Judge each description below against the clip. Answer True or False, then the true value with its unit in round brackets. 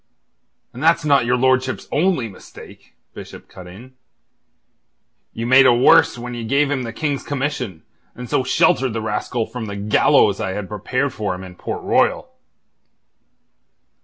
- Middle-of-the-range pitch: False (125 Hz)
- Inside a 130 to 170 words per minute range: True (160 wpm)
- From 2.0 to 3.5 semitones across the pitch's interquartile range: False (4.0 semitones)